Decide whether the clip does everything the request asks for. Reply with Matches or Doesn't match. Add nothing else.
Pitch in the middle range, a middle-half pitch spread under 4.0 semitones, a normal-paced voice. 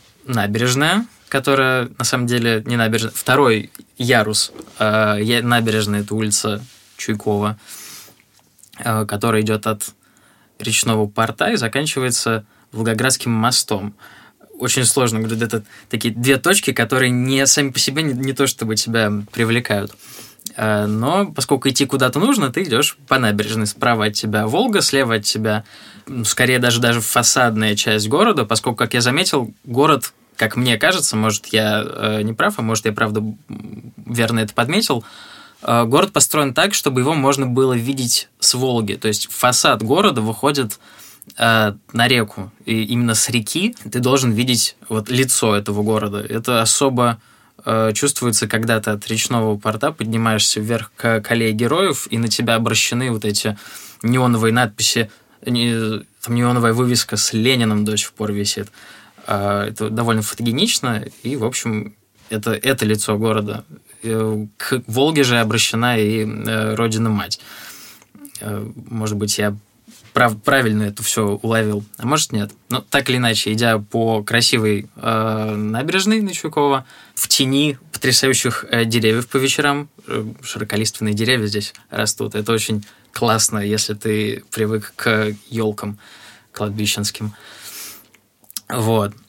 Doesn't match